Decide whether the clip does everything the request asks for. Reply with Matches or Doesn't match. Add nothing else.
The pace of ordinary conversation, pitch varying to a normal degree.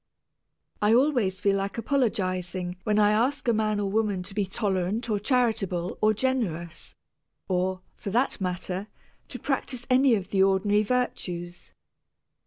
Matches